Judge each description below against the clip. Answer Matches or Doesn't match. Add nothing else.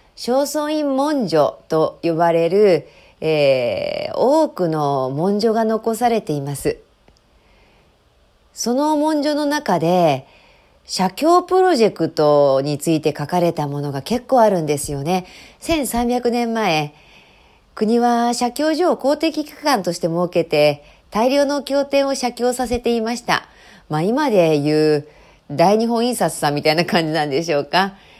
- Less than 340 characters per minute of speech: Matches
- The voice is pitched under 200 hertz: Doesn't match